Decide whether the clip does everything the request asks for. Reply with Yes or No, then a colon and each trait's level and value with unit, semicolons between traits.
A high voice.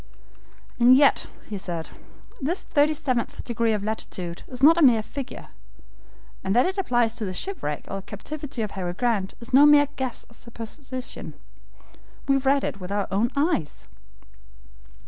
Yes: high, 240 Hz